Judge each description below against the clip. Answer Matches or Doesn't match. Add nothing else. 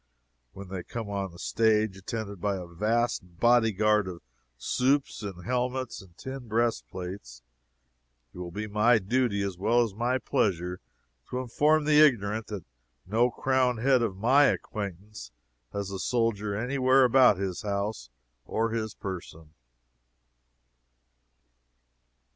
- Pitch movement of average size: Matches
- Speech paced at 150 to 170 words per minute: Doesn't match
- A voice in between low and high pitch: Doesn't match